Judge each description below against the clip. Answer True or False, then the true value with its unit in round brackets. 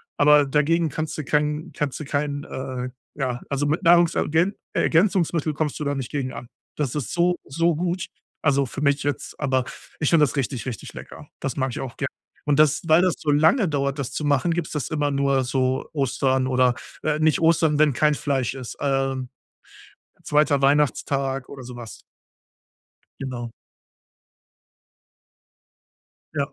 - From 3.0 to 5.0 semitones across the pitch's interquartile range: False (2.6 semitones)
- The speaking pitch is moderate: True (145 Hz)